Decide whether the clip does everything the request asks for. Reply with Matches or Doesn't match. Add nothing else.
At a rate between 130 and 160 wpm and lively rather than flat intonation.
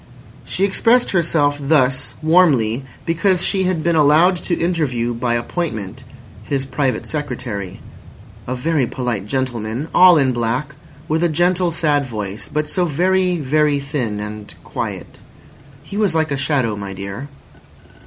Matches